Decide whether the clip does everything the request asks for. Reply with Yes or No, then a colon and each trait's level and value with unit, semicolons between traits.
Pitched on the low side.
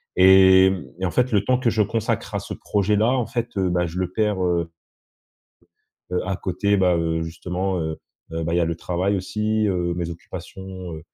Yes: very low, 95 Hz